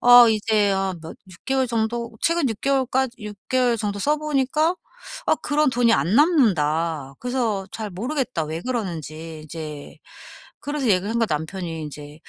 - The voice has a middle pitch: No, high, 220 Hz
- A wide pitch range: Yes, wide, 7.6 semitones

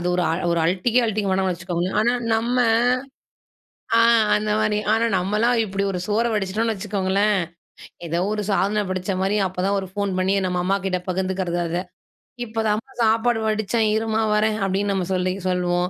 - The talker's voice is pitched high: Yes, high, 200 Hz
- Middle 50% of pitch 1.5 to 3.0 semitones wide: Yes, average, 2.7 semitones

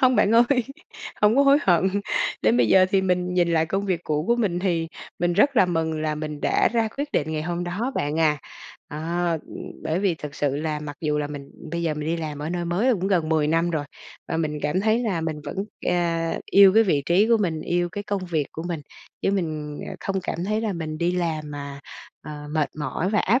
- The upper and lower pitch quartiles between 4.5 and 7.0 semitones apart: No, average, 4.1 semitones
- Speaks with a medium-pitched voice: Yes, medium, 170 Hz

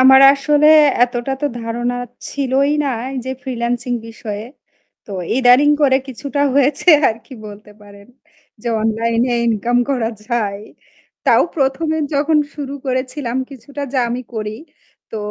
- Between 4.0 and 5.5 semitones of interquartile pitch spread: No, average, 3.2 semitones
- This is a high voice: Yes, very high, 250 Hz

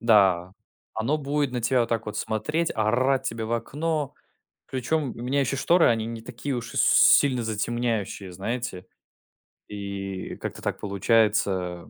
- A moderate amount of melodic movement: Yes, average, 4.2 semitones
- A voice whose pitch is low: Yes, low, 115 Hz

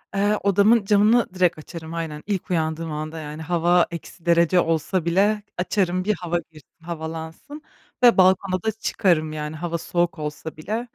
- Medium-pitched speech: Yes, medium, 175 Hz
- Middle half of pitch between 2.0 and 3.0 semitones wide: No, average, 3.5 semitones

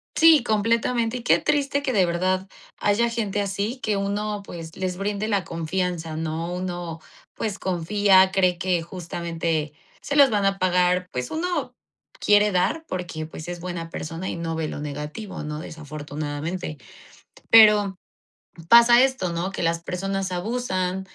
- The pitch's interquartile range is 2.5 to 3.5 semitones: No, average, 3.9 semitones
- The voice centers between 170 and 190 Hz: Yes, medium, 185 Hz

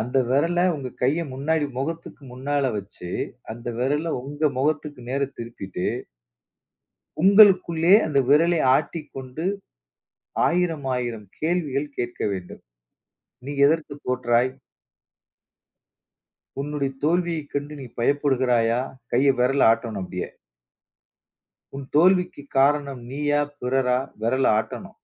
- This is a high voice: No, medium, 140 Hz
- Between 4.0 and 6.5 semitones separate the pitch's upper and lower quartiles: No, average, 3.6 semitones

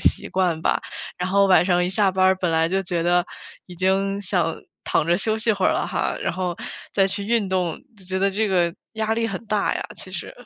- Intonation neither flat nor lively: No, narrow, 2.0 semitones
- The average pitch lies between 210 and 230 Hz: No, high, 190 Hz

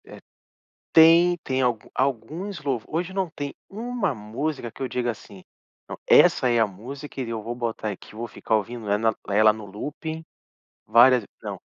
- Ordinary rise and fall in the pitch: No, wide, 5.8 semitones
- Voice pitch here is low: Yes, low, 125 Hz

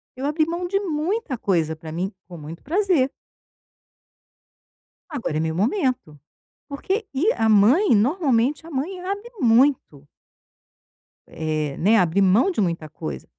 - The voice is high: Yes, very high, 250 Hz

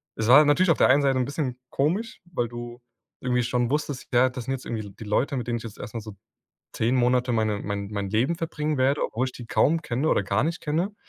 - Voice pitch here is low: Yes, low, 125 Hz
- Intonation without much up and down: No, average, 4.1 semitones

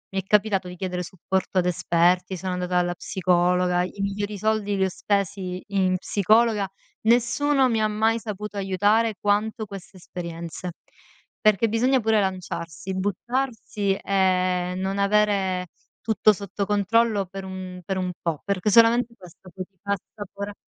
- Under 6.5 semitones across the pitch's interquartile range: Yes, narrow, 2.5 semitones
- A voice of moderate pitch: No, high, 195 Hz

